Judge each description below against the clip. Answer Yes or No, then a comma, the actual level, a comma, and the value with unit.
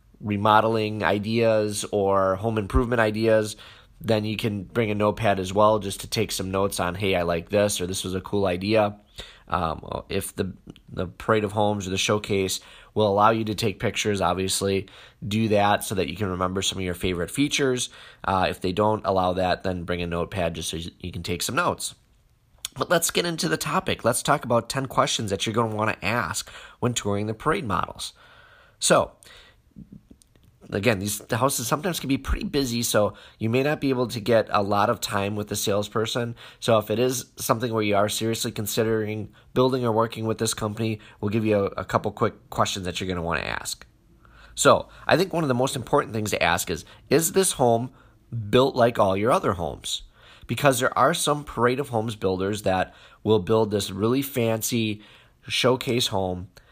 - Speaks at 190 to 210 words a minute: Yes, average, 200 wpm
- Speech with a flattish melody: No, average, 3.6 semitones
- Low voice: Yes, low, 110 Hz